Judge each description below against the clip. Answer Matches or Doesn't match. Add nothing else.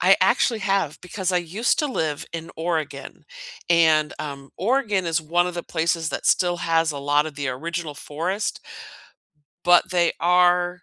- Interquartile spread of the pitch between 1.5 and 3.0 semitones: Matches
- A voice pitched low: Doesn't match